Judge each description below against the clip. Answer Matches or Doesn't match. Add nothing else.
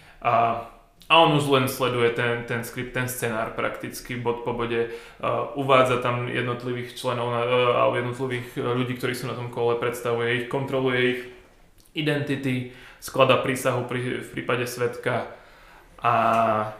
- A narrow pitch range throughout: Matches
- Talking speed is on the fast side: Doesn't match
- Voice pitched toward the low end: Matches